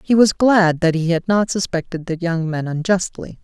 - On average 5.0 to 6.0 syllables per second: No, 4.8 syllables/s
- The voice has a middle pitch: Yes, medium, 175 Hz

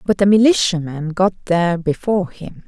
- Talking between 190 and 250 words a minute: No, average, 155 wpm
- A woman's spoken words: Yes, female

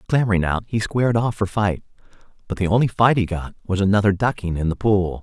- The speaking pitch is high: No, low, 100 Hz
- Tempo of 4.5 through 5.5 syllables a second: No, 6.1 syllables/s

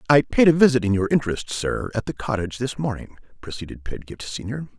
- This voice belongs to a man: Yes, male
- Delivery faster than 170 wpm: Yes, average, 200 wpm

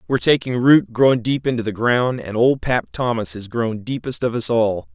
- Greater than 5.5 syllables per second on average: No, 5.1 syllables/s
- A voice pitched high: No, low, 115 Hz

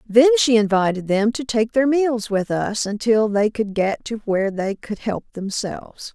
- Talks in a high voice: Yes, high, 220 Hz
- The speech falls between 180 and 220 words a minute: Yes, average, 195 wpm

